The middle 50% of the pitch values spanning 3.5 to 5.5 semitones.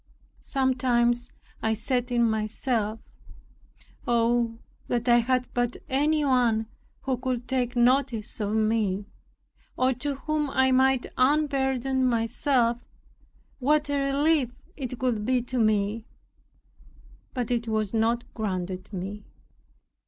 No: average, 2.7 semitones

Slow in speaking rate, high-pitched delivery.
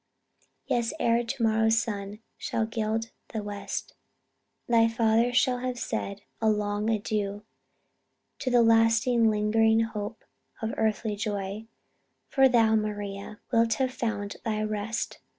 Yes: slow, 130 wpm; high, 220 Hz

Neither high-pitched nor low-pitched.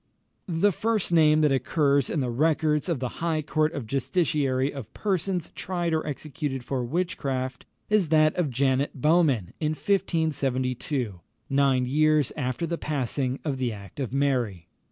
Yes: medium, 145 Hz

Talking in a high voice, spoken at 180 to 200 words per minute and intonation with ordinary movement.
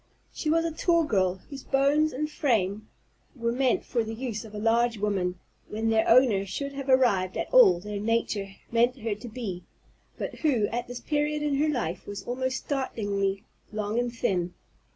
Yes: high, 230 Hz; average, 185 wpm; average, 4.9 semitones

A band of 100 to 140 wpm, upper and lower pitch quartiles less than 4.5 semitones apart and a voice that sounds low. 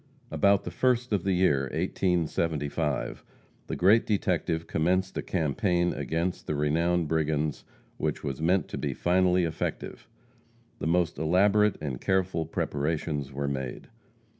Yes: slow, 135 wpm; average, 3.7 semitones; very low, 85 Hz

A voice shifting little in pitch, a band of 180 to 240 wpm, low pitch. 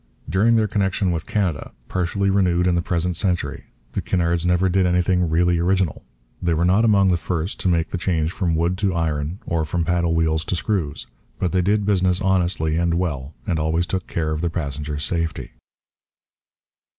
Yes: narrow, 2.3 semitones; average, 185 wpm; very low, 85 Hz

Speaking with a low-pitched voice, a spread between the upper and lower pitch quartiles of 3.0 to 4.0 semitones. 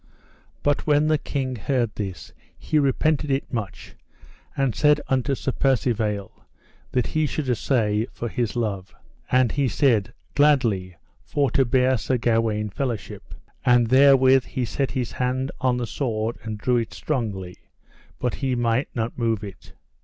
Yes: low, 125 Hz; average, 3.4 semitones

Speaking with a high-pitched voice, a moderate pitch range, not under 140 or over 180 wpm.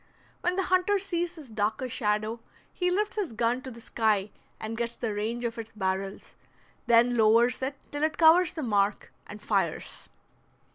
No: high, 235 Hz; wide, 6.7 semitones; average, 175 wpm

